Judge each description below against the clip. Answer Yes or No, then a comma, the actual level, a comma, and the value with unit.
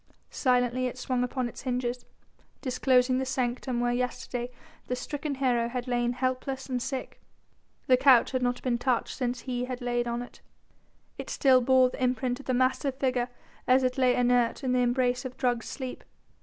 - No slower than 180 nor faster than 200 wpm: Yes, average, 185 wpm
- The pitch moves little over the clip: Yes, narrow, 0.9 semitones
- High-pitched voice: Yes, very high, 250 Hz